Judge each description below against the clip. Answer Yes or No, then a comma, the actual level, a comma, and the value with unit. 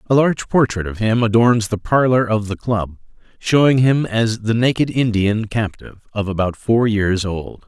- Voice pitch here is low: Yes, low, 110 Hz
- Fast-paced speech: No, average, 180 wpm